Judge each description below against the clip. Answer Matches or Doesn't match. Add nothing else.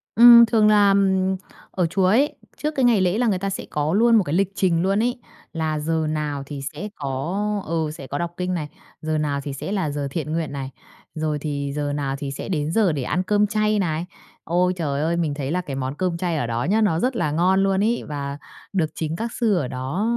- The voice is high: Doesn't match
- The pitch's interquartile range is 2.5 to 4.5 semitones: Doesn't match